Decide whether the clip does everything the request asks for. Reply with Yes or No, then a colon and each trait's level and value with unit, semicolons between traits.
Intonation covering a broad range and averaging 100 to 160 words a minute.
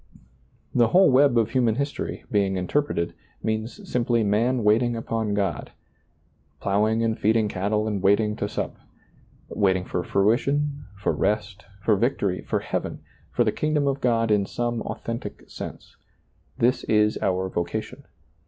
No: average, 3.0 semitones; average, 150 wpm